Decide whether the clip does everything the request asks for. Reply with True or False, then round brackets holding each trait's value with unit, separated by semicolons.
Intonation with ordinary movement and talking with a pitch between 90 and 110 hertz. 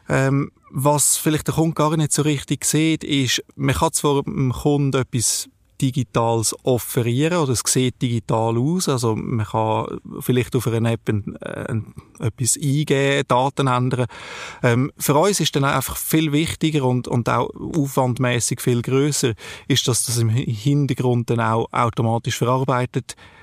False (3.3 semitones; 130 Hz)